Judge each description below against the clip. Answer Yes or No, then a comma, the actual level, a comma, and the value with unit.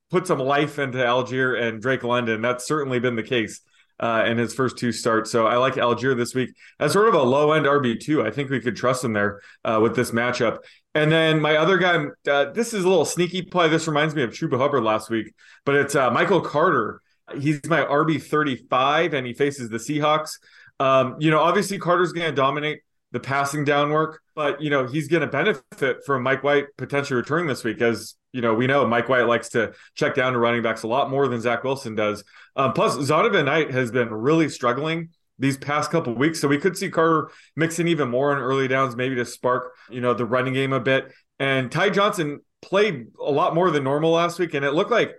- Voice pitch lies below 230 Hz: Yes, medium, 140 Hz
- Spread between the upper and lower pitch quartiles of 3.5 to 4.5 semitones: Yes, average, 3.9 semitones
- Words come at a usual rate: No, fast, 230 wpm